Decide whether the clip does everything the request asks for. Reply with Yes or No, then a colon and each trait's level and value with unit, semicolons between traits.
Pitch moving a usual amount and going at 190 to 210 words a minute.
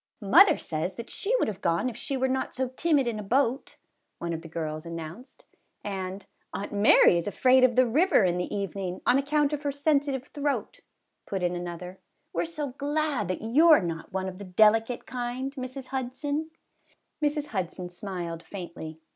No: wide, 7.3 semitones; average, 195 wpm